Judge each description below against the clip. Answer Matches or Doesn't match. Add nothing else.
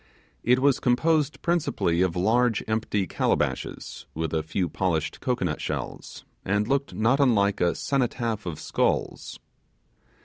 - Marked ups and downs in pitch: Matches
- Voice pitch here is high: Doesn't match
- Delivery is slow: Matches